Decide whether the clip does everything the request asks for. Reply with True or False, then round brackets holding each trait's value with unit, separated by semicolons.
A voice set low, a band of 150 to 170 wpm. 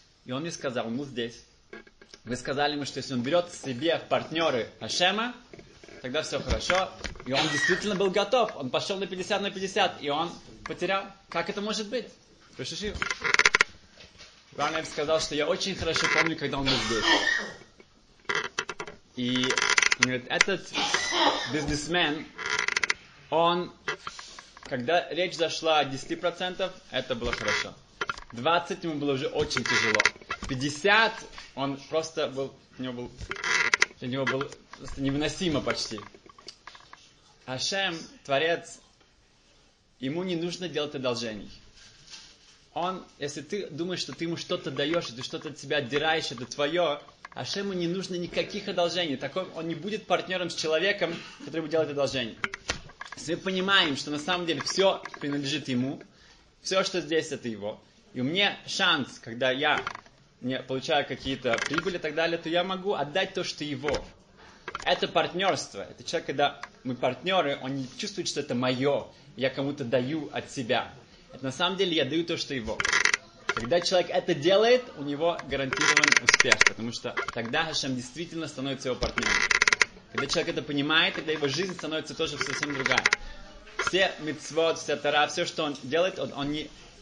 False (155 Hz; 155 wpm)